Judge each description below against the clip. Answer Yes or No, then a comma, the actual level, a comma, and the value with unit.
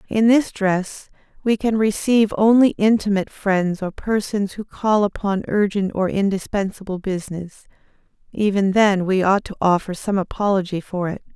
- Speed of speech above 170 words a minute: No, average, 150 wpm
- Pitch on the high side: Yes, high, 200 Hz